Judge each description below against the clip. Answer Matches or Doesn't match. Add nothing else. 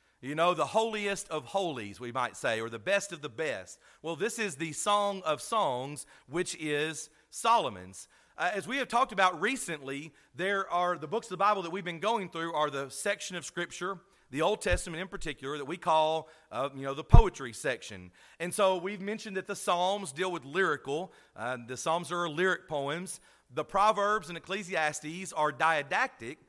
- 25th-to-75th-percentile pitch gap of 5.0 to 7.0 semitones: Doesn't match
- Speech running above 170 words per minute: Matches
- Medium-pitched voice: Matches